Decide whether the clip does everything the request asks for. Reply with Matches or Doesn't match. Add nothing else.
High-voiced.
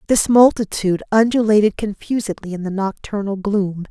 Matches